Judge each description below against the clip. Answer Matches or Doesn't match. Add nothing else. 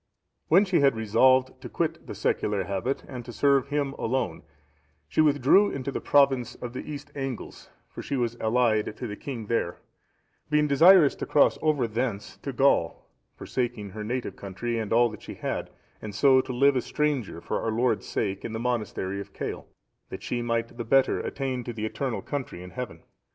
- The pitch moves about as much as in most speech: Matches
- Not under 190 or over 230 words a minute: Matches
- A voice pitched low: Matches